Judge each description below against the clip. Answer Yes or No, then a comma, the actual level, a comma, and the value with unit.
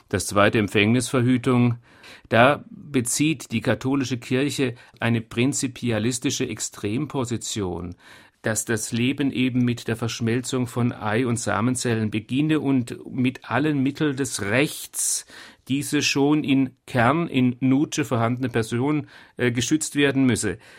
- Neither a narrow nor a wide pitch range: Yes, average, 3.0 semitones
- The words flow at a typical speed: No, slow, 115 wpm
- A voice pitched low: Yes, low, 125 Hz